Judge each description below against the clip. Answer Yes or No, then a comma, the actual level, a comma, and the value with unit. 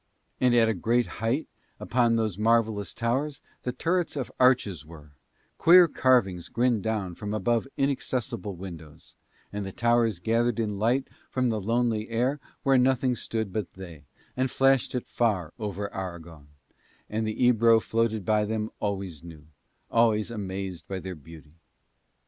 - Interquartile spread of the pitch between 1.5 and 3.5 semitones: No, average, 4.2 semitones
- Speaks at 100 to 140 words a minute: No, average, 150 wpm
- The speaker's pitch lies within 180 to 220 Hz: No, low, 110 Hz